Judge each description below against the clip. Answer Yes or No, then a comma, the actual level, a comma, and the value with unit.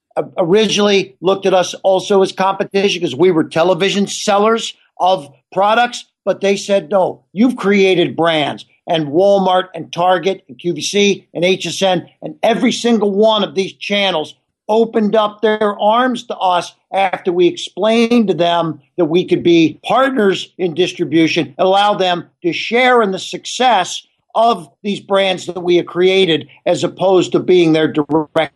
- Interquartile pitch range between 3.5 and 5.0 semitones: No, average, 3.1 semitones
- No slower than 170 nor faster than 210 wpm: No, average, 160 wpm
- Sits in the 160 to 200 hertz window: Yes, high, 190 Hz